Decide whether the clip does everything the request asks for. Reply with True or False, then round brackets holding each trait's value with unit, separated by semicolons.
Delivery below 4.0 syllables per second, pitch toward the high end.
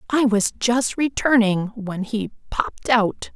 True (3.8 syllables/s; 225 Hz)